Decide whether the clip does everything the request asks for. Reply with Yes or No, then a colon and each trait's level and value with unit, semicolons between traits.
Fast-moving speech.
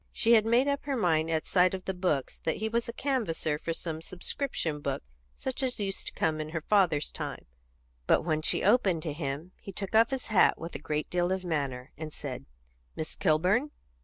Yes: fast, 215 wpm